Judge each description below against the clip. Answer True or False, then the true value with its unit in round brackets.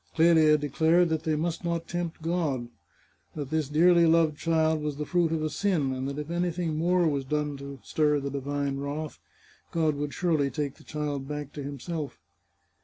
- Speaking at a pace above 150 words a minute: True (185 wpm)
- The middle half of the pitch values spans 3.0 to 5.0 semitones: False (2.5 semitones)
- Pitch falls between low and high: True (155 Hz)